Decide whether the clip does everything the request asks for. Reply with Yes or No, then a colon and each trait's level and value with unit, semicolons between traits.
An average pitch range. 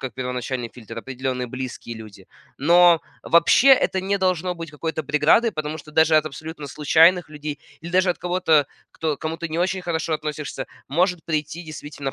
Yes: average, 3.6 semitones